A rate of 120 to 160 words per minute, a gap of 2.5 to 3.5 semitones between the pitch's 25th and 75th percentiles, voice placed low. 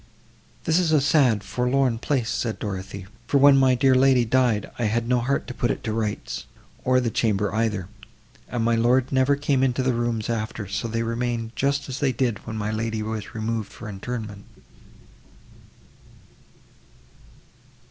No: average, 170 wpm; average, 3.0 semitones; low, 120 Hz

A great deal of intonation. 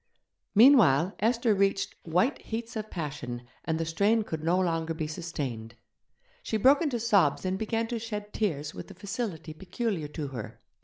Yes: wide, 6.0 semitones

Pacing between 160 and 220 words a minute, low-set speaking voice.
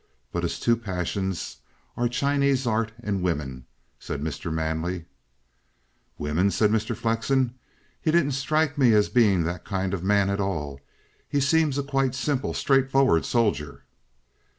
No: average, 145 wpm; low, 110 Hz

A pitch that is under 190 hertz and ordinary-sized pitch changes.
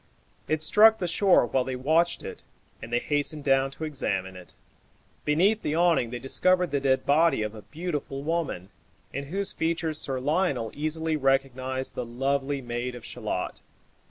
Yes: medium, 140 Hz; average, 4.3 semitones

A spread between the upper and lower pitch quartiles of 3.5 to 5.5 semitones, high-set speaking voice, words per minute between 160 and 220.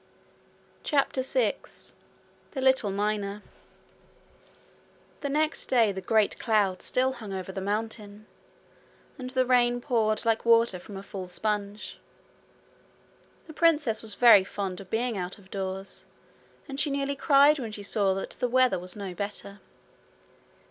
No: average, 4.4 semitones; high, 215 Hz; average, 140 wpm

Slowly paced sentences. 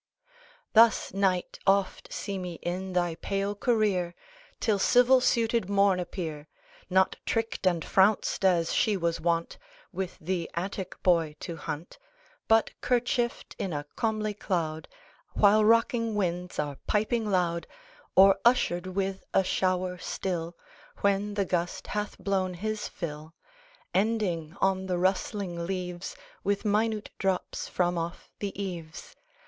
Yes: slow, 130 wpm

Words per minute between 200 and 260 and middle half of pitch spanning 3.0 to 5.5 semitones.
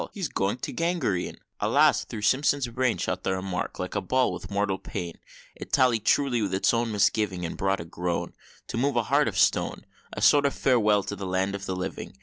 Yes: fast, 205 wpm; average, 5.1 semitones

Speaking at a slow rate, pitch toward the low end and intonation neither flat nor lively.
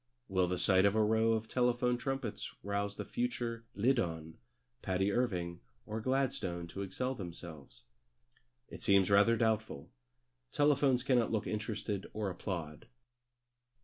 Yes: slow, 130 wpm; low, 105 Hz; average, 4.5 semitones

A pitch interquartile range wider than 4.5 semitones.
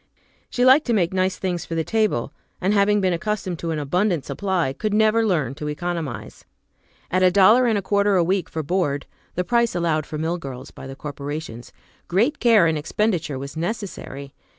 Yes: average, 5.2 semitones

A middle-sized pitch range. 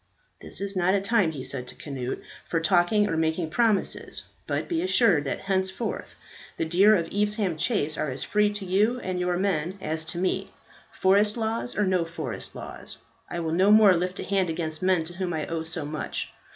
Yes: average, 3.9 semitones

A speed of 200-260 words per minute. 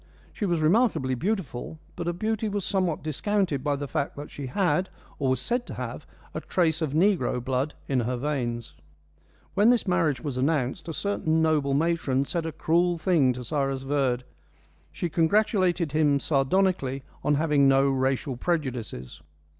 No: average, 165 wpm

